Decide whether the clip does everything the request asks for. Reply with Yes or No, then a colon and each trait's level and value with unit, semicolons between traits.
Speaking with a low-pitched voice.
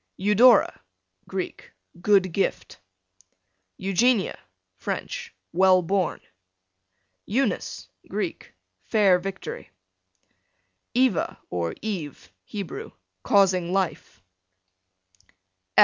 No: high, 190 Hz